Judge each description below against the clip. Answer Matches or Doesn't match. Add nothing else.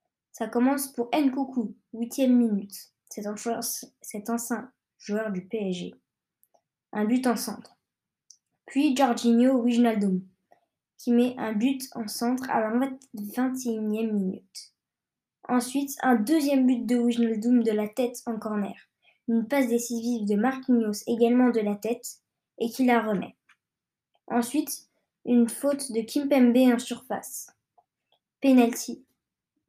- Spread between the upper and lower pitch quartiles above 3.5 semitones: Doesn't match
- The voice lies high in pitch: Matches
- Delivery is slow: Matches